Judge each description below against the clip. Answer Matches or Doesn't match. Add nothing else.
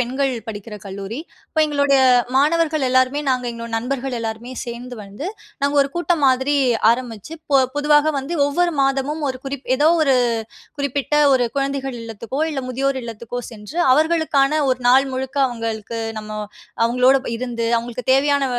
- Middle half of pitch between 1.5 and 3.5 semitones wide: Matches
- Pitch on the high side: Matches